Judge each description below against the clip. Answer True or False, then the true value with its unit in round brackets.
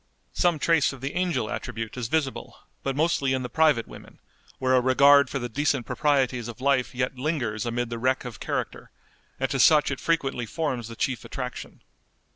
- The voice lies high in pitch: False (130 Hz)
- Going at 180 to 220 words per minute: True (190 wpm)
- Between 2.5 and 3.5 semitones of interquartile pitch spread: True (2.9 semitones)